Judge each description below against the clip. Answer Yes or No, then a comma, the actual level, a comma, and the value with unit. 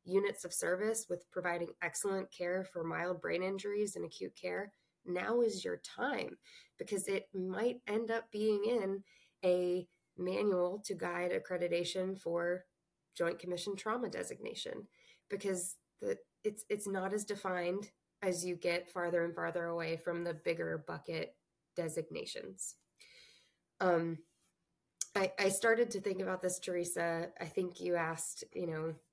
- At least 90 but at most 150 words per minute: Yes, average, 140 wpm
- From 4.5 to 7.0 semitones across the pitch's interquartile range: No, average, 2.9 semitones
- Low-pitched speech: No, medium, 185 Hz